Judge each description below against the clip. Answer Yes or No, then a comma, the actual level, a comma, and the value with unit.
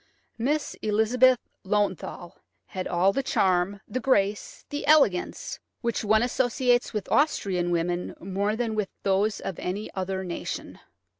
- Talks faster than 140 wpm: No, slow, 135 wpm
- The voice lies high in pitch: Yes, high, 205 Hz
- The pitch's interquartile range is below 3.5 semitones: No, average, 4.4 semitones